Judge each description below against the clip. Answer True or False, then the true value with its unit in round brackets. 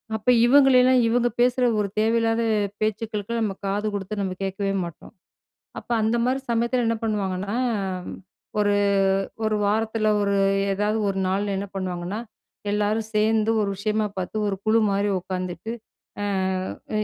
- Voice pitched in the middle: False (210 Hz)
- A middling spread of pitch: False (2.3 semitones)